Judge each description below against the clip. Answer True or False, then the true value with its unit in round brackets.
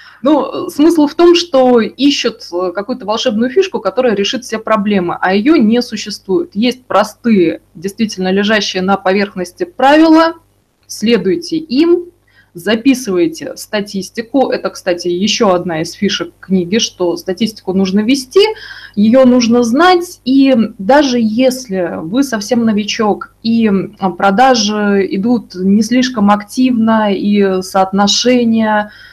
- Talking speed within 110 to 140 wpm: True (115 wpm)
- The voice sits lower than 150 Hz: False (225 Hz)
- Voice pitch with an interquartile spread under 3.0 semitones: False (5.0 semitones)